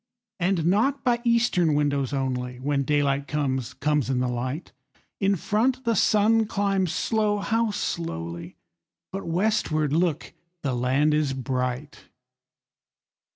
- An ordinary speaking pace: No, slow, 110 wpm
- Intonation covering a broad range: Yes, wide, 7.5 semitones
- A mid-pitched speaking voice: Yes, medium, 150 Hz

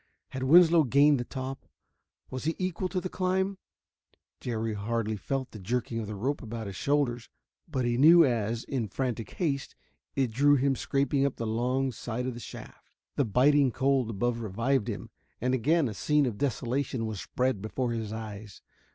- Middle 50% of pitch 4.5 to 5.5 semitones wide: No, average, 3.7 semitones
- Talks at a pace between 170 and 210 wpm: Yes, average, 180 wpm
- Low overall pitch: Yes, low, 125 Hz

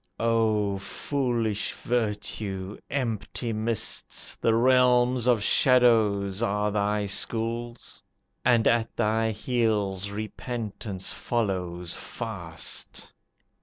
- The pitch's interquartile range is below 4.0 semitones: Yes, average, 2.7 semitones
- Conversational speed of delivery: No, slow, 85 wpm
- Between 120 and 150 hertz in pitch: No, low, 110 Hz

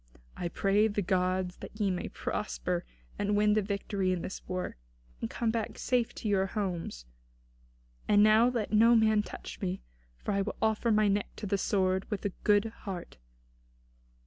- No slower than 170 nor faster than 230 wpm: Yes, average, 175 wpm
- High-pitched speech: Yes, high, 205 Hz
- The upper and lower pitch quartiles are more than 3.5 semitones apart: No, narrow, 2.4 semitones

